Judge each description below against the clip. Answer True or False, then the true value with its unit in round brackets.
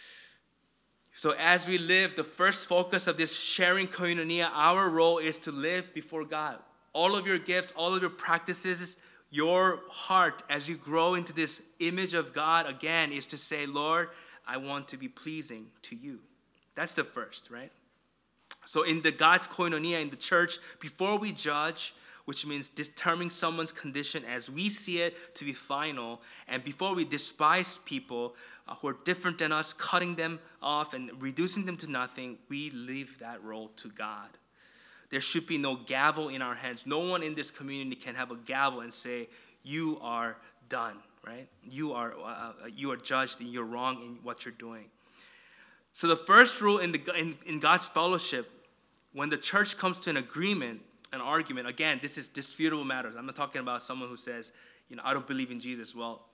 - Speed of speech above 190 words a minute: False (185 wpm)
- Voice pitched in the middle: True (155 Hz)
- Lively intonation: False (4.4 semitones)